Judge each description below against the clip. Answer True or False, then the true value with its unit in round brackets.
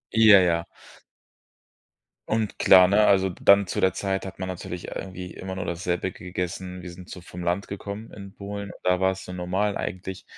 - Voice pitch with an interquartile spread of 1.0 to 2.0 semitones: True (1.6 semitones)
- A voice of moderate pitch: False (95 Hz)